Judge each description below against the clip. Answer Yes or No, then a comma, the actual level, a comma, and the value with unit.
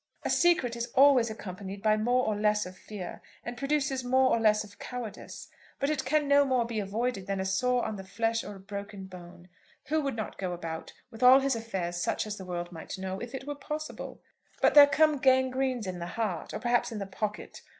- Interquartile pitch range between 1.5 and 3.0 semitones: No, average, 5.2 semitones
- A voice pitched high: Yes, high, 225 Hz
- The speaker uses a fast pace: Yes, fast, 225 wpm